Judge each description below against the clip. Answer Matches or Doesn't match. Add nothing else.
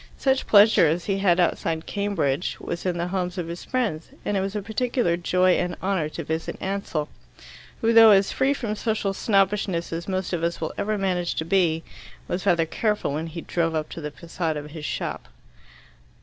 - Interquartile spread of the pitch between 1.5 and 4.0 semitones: Matches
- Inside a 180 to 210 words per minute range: Matches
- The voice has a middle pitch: Matches